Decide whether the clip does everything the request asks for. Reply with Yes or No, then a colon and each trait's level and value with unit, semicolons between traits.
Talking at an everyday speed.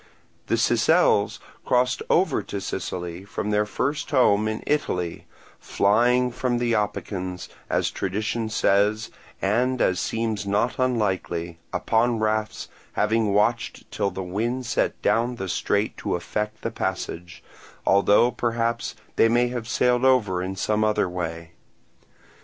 No: slow, 130 wpm